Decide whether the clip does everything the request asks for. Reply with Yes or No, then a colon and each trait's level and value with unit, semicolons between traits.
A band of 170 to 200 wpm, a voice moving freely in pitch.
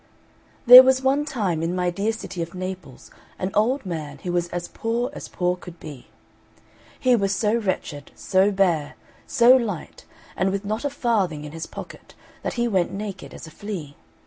No: average, 185 wpm; average, 4.8 semitones